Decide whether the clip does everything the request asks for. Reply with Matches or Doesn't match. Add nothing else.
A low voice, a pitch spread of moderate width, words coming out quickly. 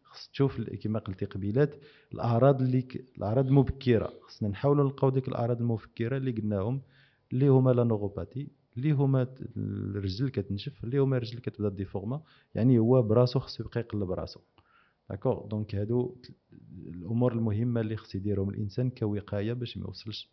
Matches